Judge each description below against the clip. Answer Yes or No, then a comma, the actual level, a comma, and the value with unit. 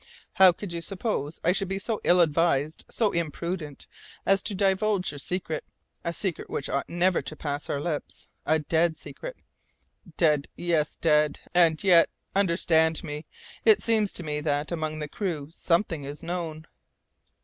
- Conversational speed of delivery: Yes, average, 160 wpm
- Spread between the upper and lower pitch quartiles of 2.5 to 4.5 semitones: Yes, average, 3.5 semitones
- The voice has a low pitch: No, medium, 170 Hz